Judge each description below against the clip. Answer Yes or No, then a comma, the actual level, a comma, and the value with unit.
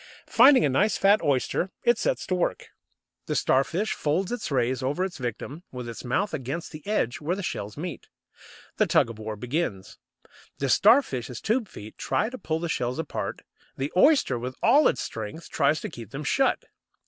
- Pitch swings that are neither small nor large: No, wide, 7.9 semitones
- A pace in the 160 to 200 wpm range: Yes, average, 185 wpm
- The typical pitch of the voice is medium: Yes, medium, 150 Hz